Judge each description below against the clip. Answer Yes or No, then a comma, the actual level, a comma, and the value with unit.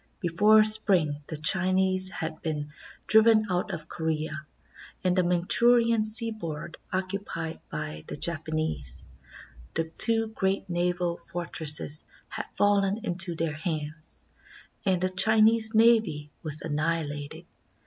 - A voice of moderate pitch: Yes, medium, 175 Hz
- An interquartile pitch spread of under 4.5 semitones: No, average, 4.8 semitones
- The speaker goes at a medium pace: No, slow, 120 wpm